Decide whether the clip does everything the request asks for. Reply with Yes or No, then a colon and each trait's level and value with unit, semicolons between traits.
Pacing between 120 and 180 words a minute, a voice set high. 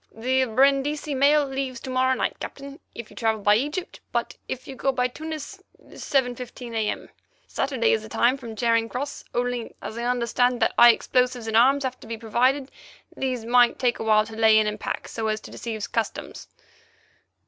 No: average, 190 wpm; high, 245 Hz